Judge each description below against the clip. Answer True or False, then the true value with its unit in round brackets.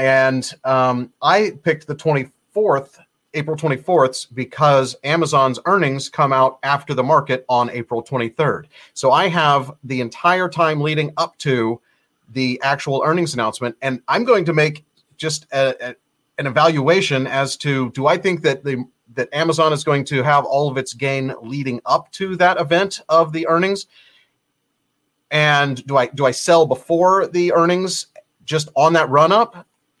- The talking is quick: False (160 wpm)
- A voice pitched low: False (145 Hz)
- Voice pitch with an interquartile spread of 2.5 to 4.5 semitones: True (3.7 semitones)